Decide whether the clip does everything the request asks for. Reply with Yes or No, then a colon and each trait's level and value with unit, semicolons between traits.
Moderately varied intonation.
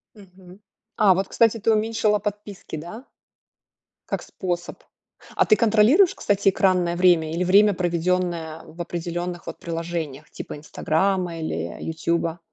Yes: average, 3.4 semitones